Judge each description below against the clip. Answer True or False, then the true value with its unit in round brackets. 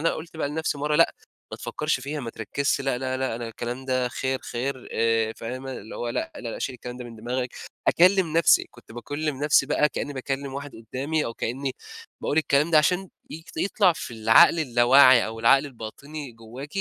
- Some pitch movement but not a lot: True (3.8 semitones)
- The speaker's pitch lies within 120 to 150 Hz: True (135 Hz)